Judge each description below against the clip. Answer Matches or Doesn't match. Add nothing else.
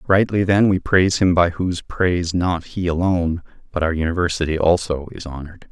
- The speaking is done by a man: Matches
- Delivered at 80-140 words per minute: Doesn't match